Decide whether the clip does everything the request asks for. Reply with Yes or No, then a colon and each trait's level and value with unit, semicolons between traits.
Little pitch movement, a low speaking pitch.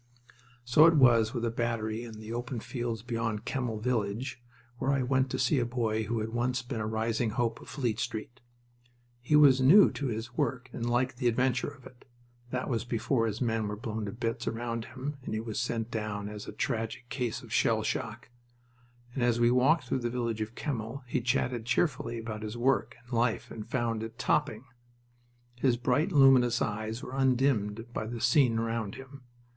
Yes: narrow, 2.3 semitones; low, 120 Hz